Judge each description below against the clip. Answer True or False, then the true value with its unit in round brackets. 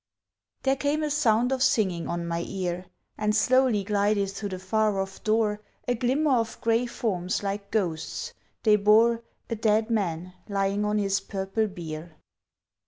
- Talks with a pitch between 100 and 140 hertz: False (210 Hz)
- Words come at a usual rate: True (160 wpm)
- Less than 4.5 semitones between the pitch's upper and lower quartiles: True (3.0 semitones)